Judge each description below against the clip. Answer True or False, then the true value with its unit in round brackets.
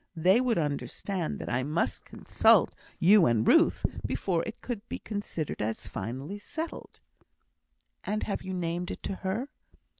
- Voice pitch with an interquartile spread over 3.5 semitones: True (5.2 semitones)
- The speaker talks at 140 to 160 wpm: True (150 wpm)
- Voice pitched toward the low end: False (185 Hz)